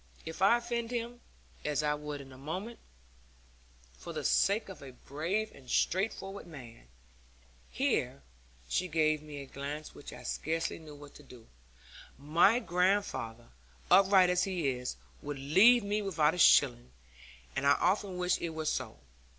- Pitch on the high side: No, medium, 160 Hz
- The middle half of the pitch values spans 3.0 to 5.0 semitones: No, wide, 5.6 semitones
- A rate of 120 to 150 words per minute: No, average, 160 wpm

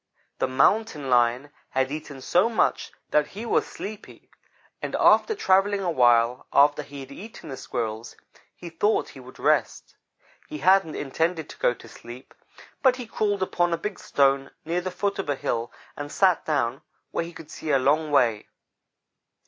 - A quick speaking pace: No, average, 175 wpm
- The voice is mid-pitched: Yes, medium, 155 Hz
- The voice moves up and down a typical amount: No, wide, 6.4 semitones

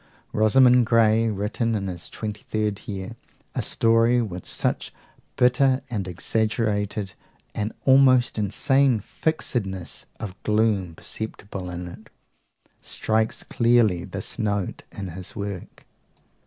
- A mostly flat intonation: No, average, 3.2 semitones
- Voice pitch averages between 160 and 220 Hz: No, low, 110 Hz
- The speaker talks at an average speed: No, slow, 115 wpm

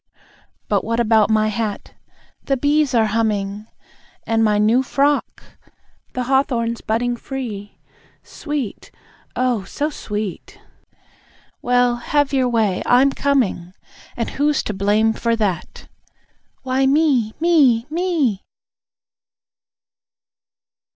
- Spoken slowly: Yes, slow, 100 wpm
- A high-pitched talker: Yes, high, 235 Hz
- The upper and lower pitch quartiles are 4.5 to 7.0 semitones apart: No, average, 4.0 semitones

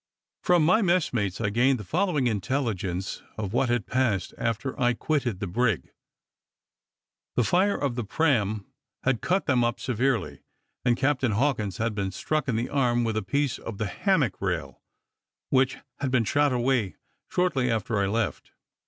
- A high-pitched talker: No, low, 120 Hz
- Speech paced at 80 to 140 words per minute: No, average, 170 wpm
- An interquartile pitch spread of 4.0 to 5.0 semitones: Yes, average, 4.6 semitones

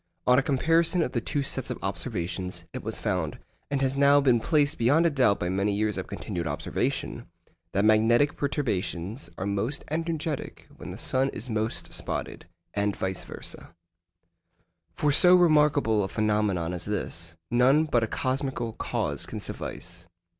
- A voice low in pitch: Yes, low, 120 Hz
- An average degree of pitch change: No, wide, 6.3 semitones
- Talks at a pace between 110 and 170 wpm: Yes, average, 160 wpm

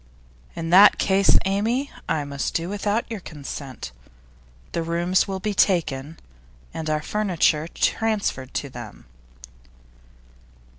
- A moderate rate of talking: No, slow, 115 wpm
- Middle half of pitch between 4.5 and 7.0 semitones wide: Yes, average, 5.2 semitones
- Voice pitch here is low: No, medium, 170 Hz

